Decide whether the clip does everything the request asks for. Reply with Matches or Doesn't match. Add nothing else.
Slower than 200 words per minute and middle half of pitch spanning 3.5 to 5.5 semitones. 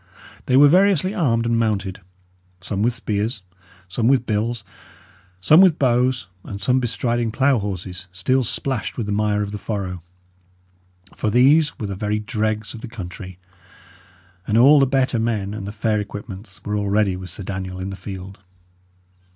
Matches